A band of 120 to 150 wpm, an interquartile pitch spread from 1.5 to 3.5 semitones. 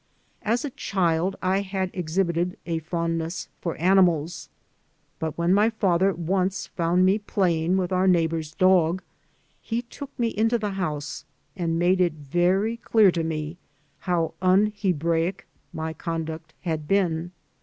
Yes: average, 145 wpm; average, 2.8 semitones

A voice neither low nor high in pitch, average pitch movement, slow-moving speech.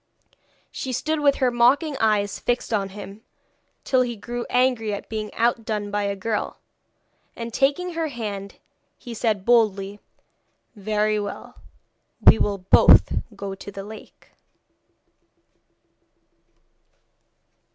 No: high, 220 Hz; average, 3.1 semitones; slow, 120 wpm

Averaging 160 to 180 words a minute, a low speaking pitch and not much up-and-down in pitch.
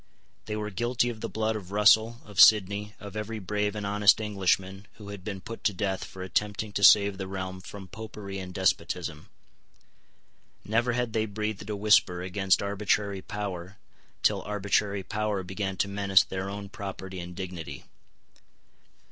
Yes: average, 165 wpm; low, 100 Hz; narrow, 2.0 semitones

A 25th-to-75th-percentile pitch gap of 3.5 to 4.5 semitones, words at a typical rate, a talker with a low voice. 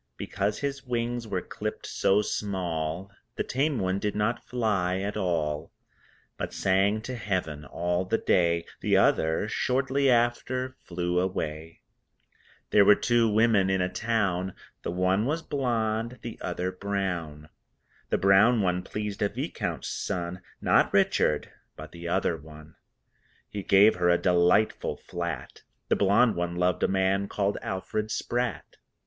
Yes: average, 4.0 semitones; average, 145 wpm; very low, 95 Hz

